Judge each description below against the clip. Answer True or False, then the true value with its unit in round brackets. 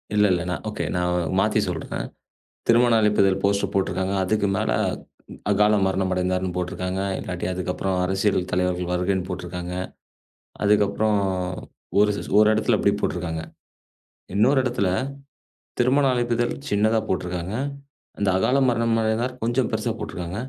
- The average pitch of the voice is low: True (100 Hz)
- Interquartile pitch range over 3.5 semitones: False (3.2 semitones)